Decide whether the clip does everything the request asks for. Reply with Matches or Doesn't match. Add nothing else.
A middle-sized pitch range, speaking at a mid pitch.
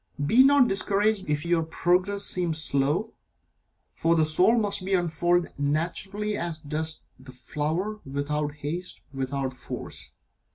Matches